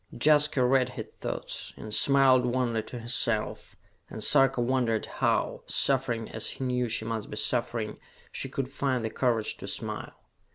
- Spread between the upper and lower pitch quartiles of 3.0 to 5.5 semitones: No, narrow, 2.6 semitones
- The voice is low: Yes, low, 125 Hz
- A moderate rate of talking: Yes, average, 160 wpm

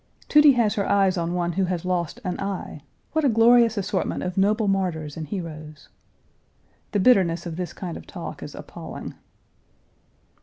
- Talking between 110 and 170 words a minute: Yes, average, 165 wpm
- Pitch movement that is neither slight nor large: Yes, average, 3.7 semitones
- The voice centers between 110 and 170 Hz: No, medium, 185 Hz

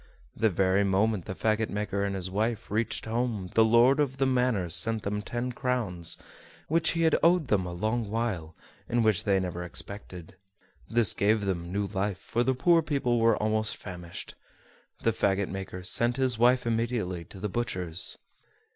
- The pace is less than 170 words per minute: No, average, 175 wpm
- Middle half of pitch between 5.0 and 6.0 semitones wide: No, average, 3.9 semitones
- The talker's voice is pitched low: Yes, low, 110 Hz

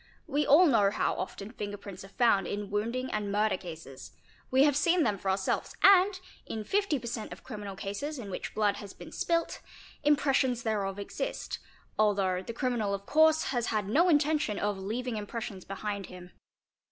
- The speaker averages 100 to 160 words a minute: No, average, 180 wpm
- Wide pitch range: Yes, wide, 5.7 semitones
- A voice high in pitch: Yes, high, 215 Hz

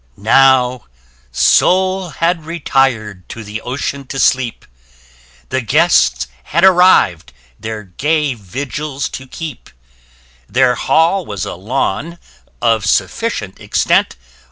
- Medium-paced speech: No, slow, 105 wpm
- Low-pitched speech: Yes, low, 130 Hz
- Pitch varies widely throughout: Yes, wide, 6.7 semitones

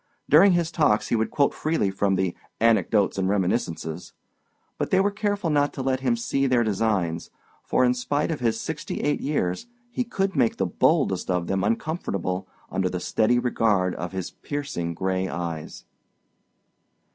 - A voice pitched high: No, low, 115 Hz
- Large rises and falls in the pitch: Yes, wide, 7.7 semitones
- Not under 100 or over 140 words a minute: No, average, 170 wpm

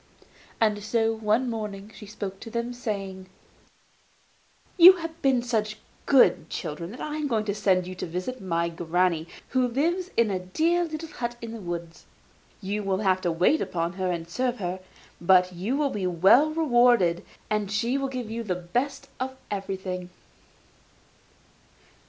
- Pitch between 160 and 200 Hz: No, high, 210 Hz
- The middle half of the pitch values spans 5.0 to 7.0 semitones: Yes, average, 5.3 semitones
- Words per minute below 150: No, average, 165 wpm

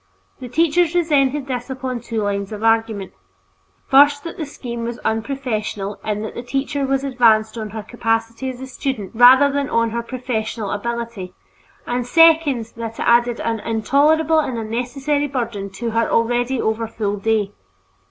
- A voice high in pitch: Yes, high, 235 Hz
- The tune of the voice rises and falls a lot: No, average, 3.5 semitones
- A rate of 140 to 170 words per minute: Yes, average, 160 wpm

